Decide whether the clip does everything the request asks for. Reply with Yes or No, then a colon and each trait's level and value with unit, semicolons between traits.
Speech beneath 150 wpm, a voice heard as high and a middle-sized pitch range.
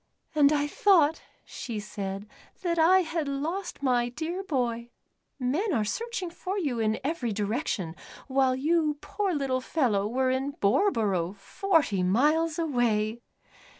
No: slow, 135 wpm; very high, 275 Hz; wide, 6.4 semitones